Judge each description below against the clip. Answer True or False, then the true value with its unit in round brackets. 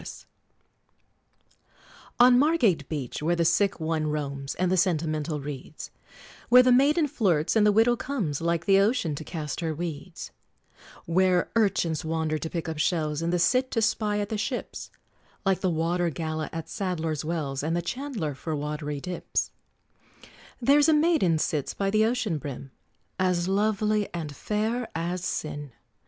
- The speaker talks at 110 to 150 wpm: False (160 wpm)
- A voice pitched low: False (175 Hz)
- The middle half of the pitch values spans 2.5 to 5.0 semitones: False (5.4 semitones)